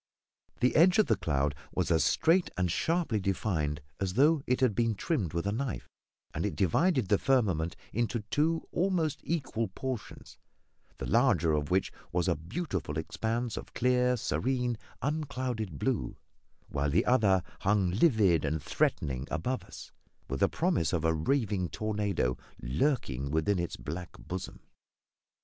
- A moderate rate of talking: Yes, average, 150 wpm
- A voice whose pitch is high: No, low, 105 Hz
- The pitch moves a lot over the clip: Yes, wide, 7.9 semitones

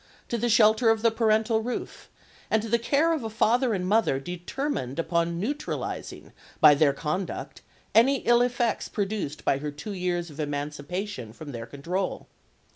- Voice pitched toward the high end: Yes, high, 200 Hz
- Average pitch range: No, wide, 7.1 semitones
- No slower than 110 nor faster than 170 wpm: Yes, average, 165 wpm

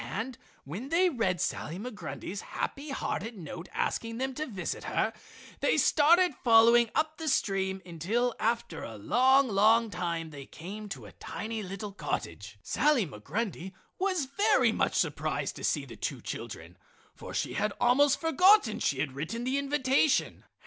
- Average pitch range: No, wide, 6.7 semitones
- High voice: Yes, high, 230 Hz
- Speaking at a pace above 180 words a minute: No, average, 155 wpm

